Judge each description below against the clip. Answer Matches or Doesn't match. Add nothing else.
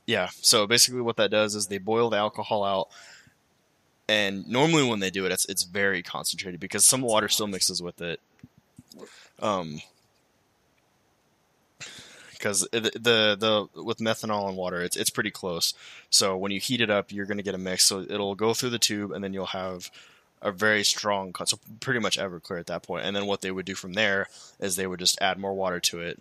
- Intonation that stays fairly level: Matches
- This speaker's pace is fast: Matches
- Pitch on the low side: Matches